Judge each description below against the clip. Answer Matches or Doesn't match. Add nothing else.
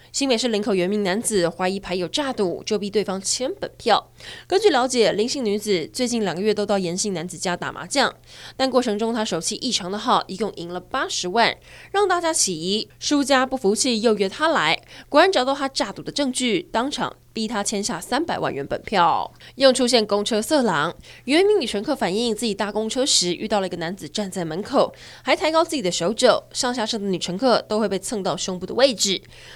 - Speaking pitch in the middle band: Doesn't match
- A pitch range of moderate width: Matches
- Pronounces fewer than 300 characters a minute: Doesn't match